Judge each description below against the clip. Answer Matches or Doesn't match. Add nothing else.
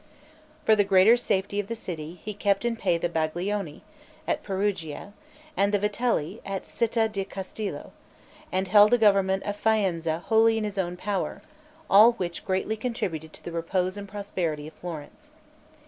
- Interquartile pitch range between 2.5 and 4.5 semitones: Matches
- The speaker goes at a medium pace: Matches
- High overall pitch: Matches